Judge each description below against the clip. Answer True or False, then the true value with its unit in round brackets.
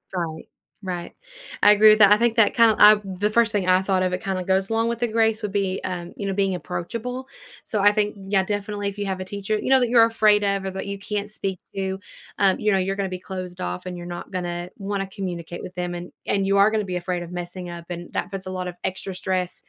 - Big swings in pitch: False (2.4 semitones)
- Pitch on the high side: True (195 Hz)